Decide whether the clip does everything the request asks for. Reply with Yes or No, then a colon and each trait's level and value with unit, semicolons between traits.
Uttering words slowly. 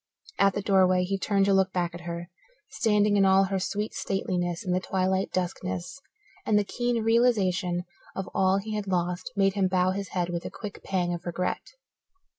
No: average, 195 wpm